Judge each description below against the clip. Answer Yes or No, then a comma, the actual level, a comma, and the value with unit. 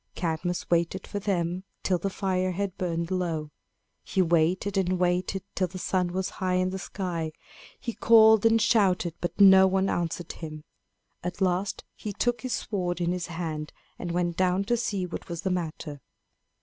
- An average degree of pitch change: No, narrow, 2.0 semitones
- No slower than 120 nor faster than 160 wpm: No, average, 175 wpm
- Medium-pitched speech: Yes, medium, 180 Hz